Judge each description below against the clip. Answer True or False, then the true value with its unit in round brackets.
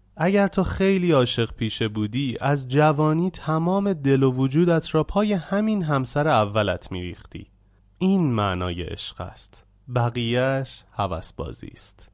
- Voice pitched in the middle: False (130 Hz)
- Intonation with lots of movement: True (7.6 semitones)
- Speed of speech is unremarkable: True (125 wpm)